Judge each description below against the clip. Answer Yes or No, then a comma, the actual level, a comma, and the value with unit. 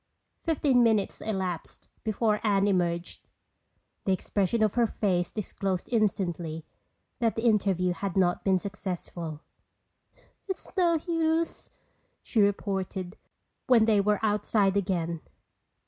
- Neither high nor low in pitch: No, high, 200 Hz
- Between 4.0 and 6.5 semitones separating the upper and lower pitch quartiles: No, average, 3.5 semitones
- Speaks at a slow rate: Yes, slow, 115 wpm